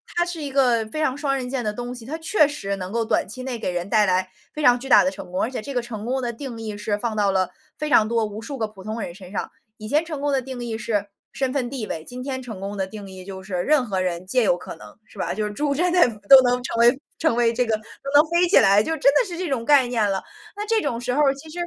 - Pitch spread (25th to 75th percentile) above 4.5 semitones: Yes, average, 4.9 semitones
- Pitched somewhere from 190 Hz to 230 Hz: No, high, 240 Hz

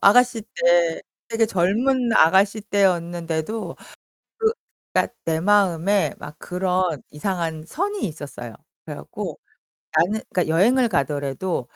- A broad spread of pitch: No, average, 4.6 semitones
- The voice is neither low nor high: Yes, medium, 180 Hz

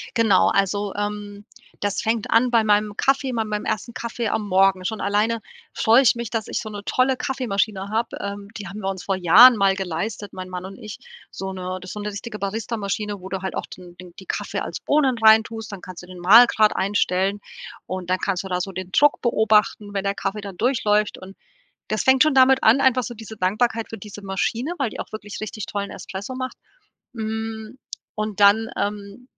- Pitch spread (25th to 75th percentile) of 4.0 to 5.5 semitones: No, narrow, 2.6 semitones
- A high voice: Yes, high, 210 Hz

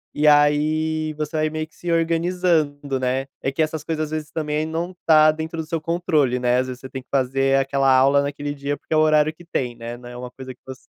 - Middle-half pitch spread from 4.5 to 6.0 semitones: No, average, 2.8 semitones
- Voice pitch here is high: No, medium, 150 Hz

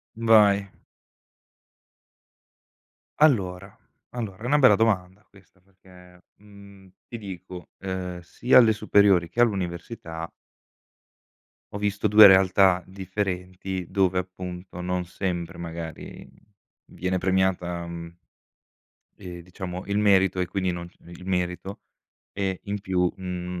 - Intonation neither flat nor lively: No, narrow, 2.0 semitones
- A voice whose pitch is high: No, very low, 95 Hz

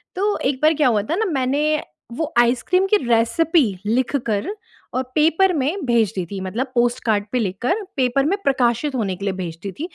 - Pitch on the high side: Yes, very high, 255 Hz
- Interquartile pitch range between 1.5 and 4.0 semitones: No, wide, 5.5 semitones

